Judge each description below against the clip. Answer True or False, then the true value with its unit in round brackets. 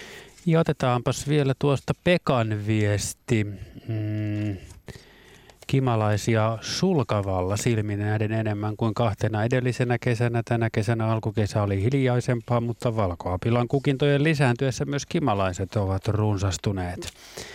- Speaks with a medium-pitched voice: False (115 Hz)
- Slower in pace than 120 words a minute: True (100 wpm)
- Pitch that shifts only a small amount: False (3.5 semitones)